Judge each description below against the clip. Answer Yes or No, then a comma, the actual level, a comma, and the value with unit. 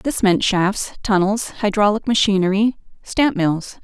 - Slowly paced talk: Yes, slow, 125 wpm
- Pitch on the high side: Yes, high, 205 Hz